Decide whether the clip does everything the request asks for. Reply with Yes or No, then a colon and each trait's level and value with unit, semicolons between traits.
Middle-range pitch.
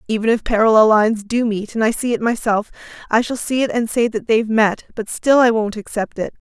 No: high, 225 Hz